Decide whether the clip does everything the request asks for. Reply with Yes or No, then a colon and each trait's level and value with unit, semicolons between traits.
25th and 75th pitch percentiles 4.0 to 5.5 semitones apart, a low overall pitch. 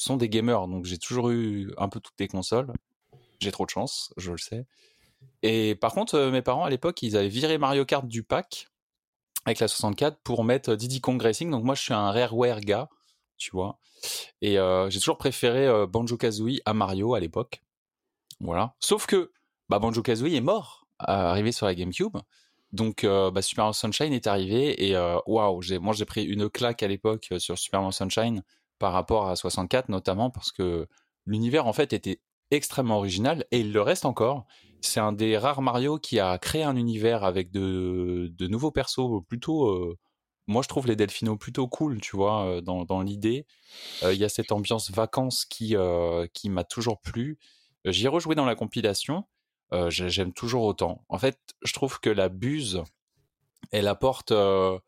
Yes: average, 4.7 semitones; low, 110 Hz